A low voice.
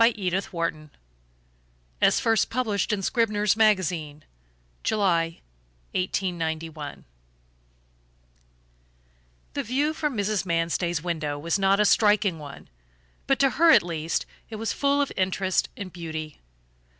No: high, 190 Hz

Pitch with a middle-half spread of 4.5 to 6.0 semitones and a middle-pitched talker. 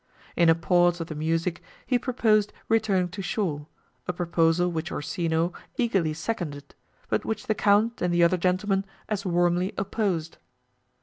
No: average, 3.5 semitones; medium, 175 Hz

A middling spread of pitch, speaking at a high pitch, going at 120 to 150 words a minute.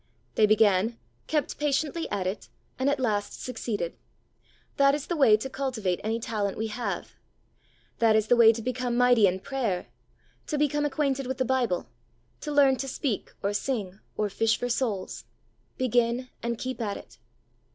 No: average, 3.9 semitones; high, 240 Hz; average, 170 wpm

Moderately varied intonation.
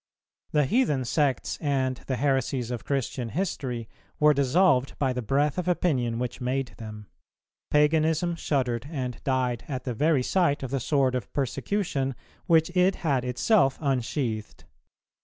Yes: average, 3.3 semitones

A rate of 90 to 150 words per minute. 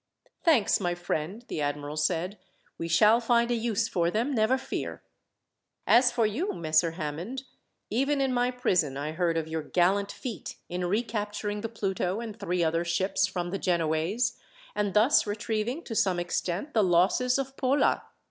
No: average, 165 wpm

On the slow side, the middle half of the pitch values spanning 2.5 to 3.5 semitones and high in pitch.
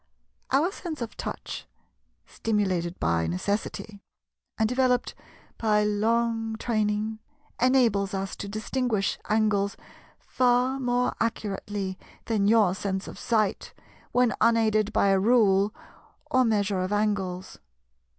Yes: slow, 110 wpm; average, 2.8 semitones; high, 215 Hz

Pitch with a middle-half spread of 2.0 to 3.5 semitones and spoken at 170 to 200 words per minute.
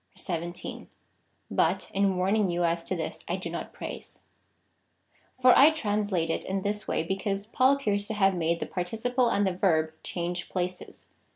Yes: average, 3.2 semitones; average, 175 wpm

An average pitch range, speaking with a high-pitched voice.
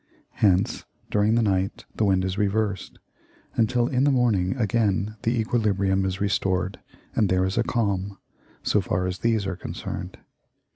No: average, 3.0 semitones; low, 100 Hz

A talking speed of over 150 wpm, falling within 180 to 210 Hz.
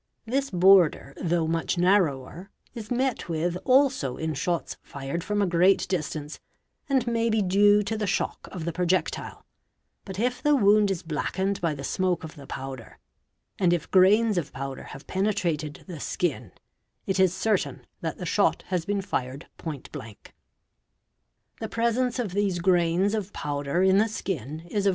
Yes: average, 175 wpm; medium, 185 Hz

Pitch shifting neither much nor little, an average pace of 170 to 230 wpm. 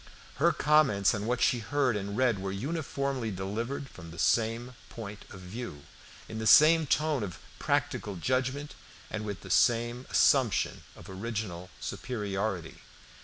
No: average, 4.8 semitones; average, 145 wpm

